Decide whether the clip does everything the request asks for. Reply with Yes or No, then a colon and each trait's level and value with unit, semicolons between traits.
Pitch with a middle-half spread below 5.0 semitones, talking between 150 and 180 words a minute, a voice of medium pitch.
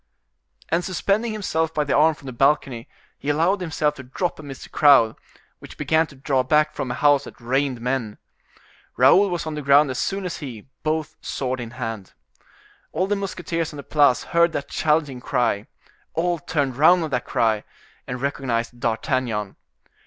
Yes: average, 4.2 semitones; average, 175 wpm; medium, 145 Hz